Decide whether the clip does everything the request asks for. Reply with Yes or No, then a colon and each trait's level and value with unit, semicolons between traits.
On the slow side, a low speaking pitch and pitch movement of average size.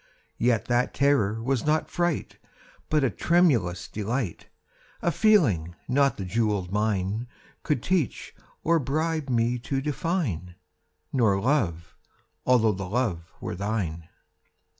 No: slow, 120 wpm; low, 115 Hz; wide, 6.7 semitones